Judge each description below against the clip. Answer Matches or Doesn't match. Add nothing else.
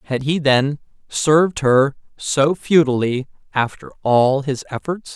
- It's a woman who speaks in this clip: Doesn't match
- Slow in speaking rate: Matches